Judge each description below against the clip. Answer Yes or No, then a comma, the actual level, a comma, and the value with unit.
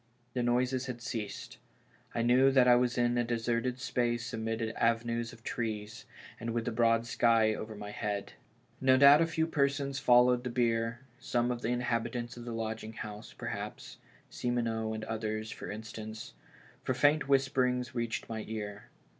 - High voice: No, low, 120 Hz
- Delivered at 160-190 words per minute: Yes, average, 170 wpm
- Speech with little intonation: Yes, narrow, 1.9 semitones